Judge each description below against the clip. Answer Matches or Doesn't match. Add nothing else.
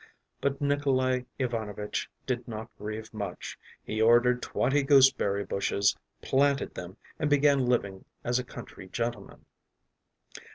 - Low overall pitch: Matches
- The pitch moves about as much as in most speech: Matches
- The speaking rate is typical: Doesn't match